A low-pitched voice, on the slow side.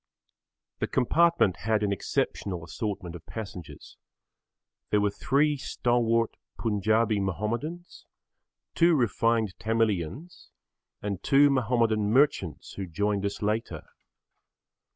Yes: low, 110 Hz; slow, 100 wpm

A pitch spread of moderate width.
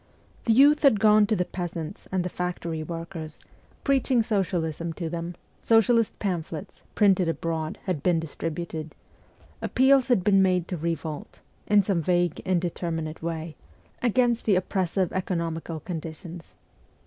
Yes: average, 3.7 semitones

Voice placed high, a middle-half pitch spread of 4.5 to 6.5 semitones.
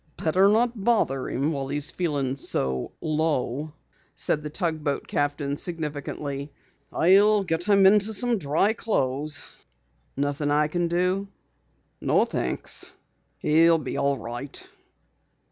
No: medium, 155 Hz; average, 4.8 semitones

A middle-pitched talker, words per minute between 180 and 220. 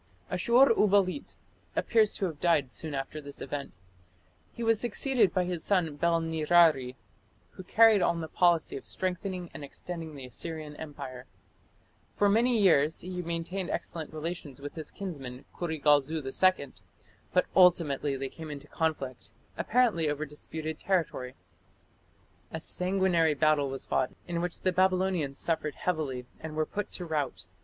No: medium, 165 Hz; average, 150 wpm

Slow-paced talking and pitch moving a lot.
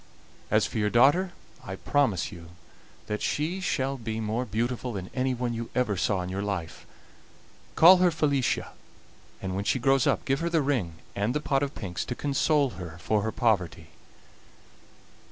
No: average, 170 wpm; wide, 5.7 semitones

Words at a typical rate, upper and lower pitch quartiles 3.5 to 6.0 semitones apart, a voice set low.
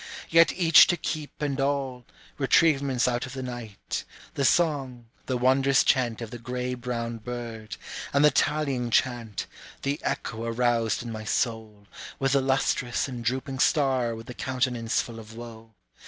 No: average, 160 wpm; average, 2.7 semitones; low, 125 Hz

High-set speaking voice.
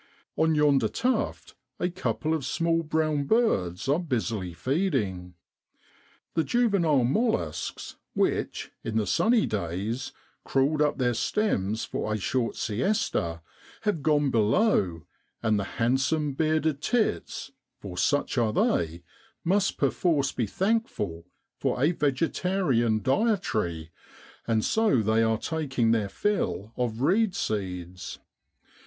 No: low, 135 Hz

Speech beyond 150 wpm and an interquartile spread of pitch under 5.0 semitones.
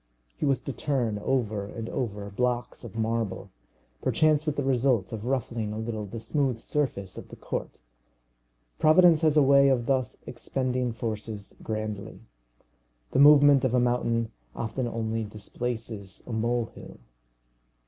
No: average, 145 wpm; average, 3.5 semitones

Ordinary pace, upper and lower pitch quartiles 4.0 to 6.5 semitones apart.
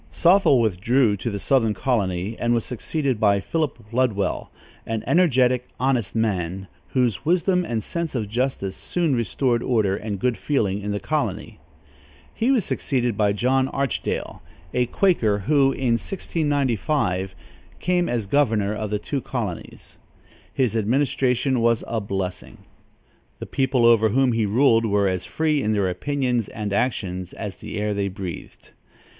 Yes: average, 150 wpm; average, 4.7 semitones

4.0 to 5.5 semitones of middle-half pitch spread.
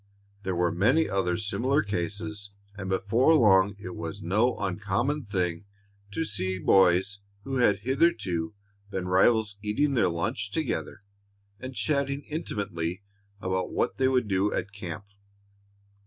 Yes: average, 4.5 semitones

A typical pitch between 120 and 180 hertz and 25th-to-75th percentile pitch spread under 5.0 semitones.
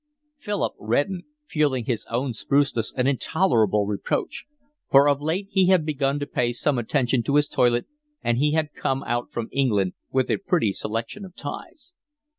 Yes: low, 135 Hz; average, 4.4 semitones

